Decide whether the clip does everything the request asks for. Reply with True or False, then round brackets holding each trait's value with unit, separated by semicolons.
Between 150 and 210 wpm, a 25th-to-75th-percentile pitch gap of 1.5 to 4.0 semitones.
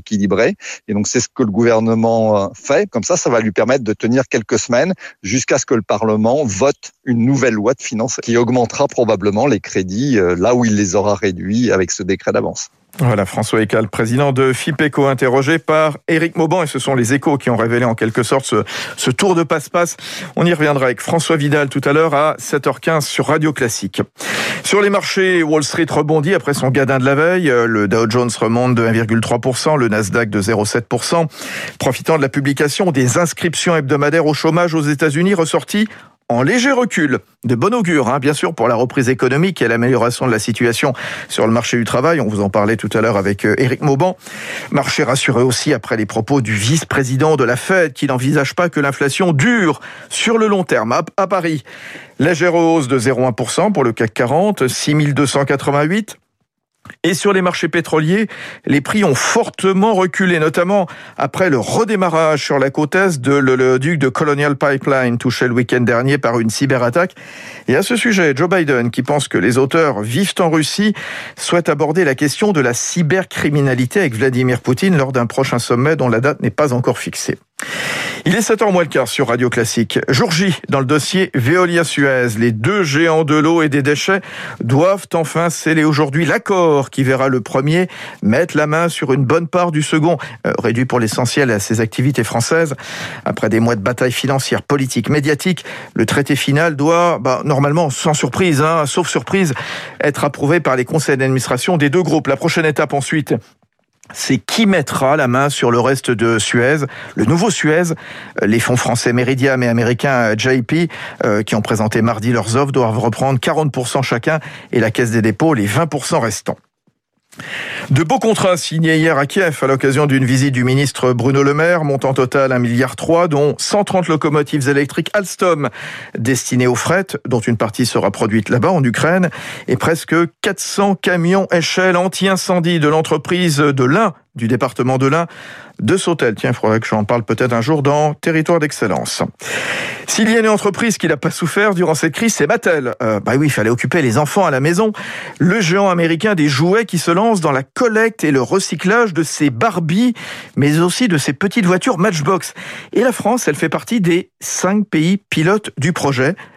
False (190 wpm; 5.3 semitones)